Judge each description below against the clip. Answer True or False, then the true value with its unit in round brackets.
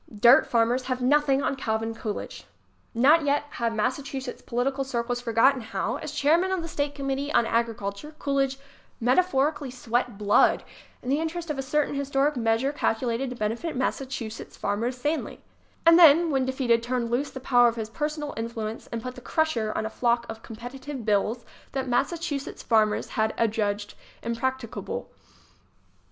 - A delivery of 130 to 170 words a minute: True (165 wpm)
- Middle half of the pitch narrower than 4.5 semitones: True (3.6 semitones)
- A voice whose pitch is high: True (255 Hz)